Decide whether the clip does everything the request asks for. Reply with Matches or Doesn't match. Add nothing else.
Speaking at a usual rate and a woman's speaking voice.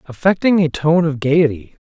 Doesn't match